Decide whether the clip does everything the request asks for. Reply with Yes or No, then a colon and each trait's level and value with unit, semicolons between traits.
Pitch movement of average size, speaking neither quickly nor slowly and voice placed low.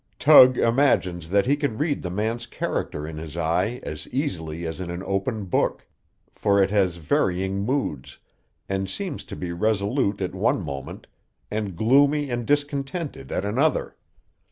No: wide, 7.2 semitones; average, 155 wpm; low, 100 Hz